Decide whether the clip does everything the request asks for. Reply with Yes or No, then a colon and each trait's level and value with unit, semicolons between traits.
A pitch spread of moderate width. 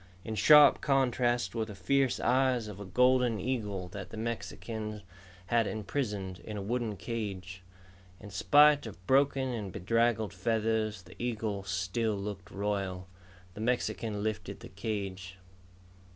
Yes: average, 3.5 semitones